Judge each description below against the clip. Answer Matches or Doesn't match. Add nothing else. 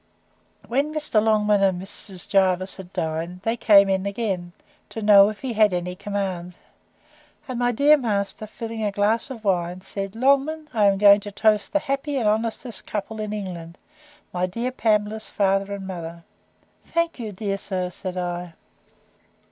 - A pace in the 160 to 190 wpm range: Matches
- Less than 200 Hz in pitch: Doesn't match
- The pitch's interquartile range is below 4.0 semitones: Matches